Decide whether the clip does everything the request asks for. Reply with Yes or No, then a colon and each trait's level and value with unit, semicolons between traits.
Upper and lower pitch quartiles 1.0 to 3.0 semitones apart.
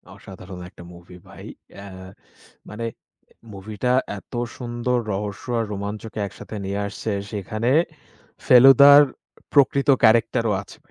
No: average, 3.8 semitones